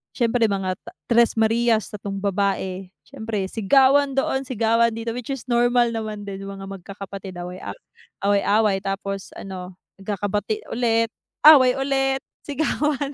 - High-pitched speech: Yes, high, 220 Hz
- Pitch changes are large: No, average, 3.7 semitones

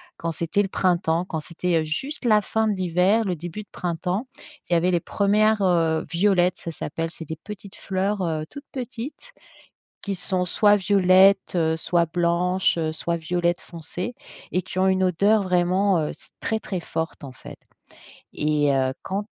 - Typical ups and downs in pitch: Yes, average, 3.1 semitones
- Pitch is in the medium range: Yes, medium, 180 Hz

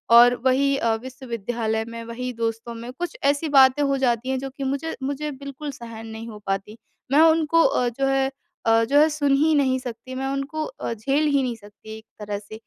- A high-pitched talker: Yes, very high, 260 Hz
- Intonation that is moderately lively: Yes, average, 3.6 semitones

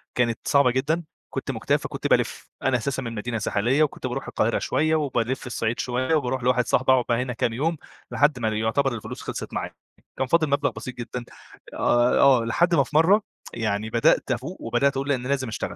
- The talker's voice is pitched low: Yes, low, 130 Hz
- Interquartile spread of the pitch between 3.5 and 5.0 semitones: No, average, 3.0 semitones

